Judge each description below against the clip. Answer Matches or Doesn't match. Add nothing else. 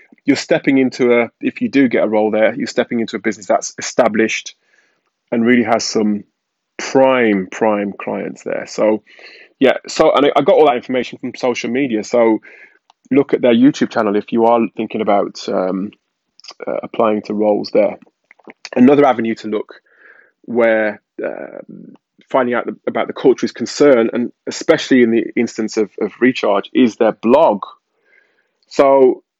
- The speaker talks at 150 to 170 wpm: Matches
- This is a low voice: Matches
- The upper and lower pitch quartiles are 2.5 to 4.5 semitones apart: Matches